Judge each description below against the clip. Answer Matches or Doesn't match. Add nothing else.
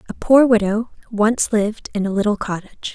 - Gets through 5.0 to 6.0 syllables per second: Matches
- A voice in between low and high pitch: Doesn't match